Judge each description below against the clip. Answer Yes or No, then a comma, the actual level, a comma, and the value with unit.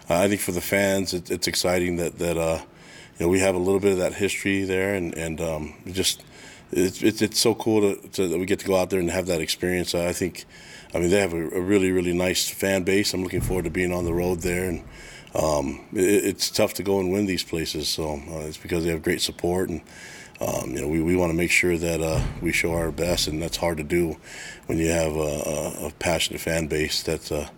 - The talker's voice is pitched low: Yes, very low, 90 Hz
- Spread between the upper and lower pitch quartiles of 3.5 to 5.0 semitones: No, average, 2.7 semitones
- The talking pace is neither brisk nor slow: No, fast, 255 wpm